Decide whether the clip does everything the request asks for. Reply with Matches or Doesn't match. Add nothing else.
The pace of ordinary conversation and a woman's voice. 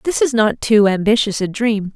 Doesn't match